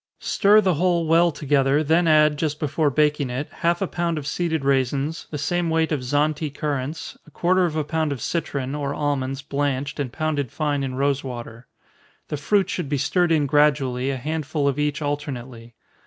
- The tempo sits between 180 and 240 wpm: Yes, average, 185 wpm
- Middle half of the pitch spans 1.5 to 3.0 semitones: Yes, average, 2.7 semitones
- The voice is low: No, medium, 150 Hz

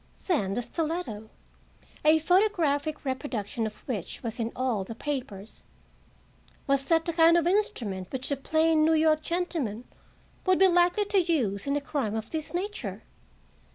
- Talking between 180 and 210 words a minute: No, average, 150 wpm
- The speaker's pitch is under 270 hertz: No, very high, 290 Hz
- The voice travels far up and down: Yes, wide, 6.8 semitones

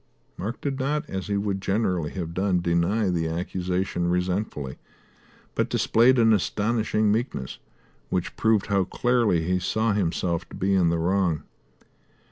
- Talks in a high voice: No, very low, 95 Hz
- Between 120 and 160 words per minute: Yes, average, 145 wpm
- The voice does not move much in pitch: No, average, 3.7 semitones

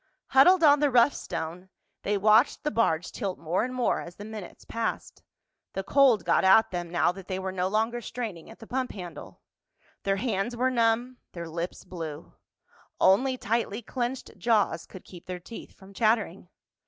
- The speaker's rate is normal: Yes, average, 180 wpm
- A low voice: No, high, 210 Hz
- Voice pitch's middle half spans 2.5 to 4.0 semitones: No, average, 4.8 semitones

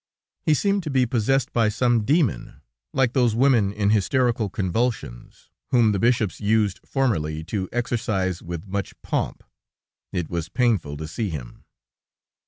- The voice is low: Yes, low, 110 Hz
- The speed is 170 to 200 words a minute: No, average, 145 wpm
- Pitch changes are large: No, average, 4.8 semitones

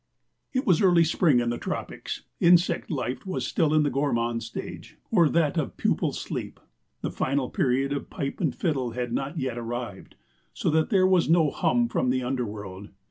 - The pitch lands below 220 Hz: Yes, medium, 140 Hz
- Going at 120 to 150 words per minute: No, average, 185 wpm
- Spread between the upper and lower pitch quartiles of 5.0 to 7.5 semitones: Yes, wide, 5.5 semitones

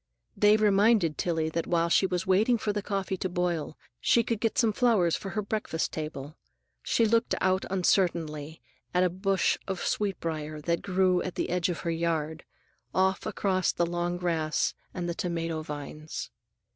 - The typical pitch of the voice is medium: Yes, medium, 180 Hz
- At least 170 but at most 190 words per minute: Yes, average, 175 wpm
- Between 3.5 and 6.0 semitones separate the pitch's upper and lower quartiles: No, average, 3.0 semitones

